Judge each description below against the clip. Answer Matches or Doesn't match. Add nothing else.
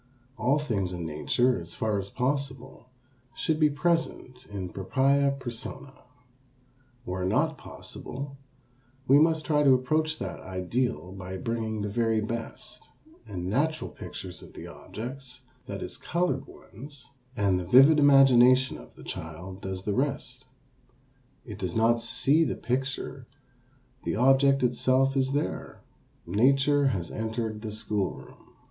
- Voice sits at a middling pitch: Doesn't match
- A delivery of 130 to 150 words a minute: Matches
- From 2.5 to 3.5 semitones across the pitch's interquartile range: Doesn't match